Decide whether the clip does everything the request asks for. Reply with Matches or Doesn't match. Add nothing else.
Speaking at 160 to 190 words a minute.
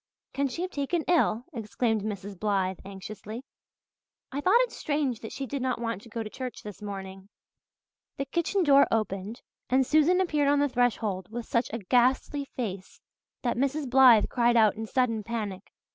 Matches